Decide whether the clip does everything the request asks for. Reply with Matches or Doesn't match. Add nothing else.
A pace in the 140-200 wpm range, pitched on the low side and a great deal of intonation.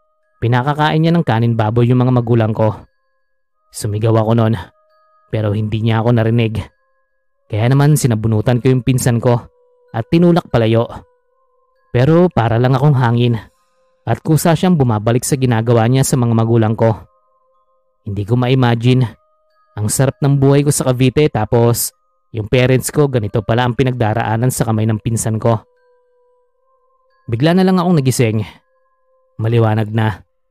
Matches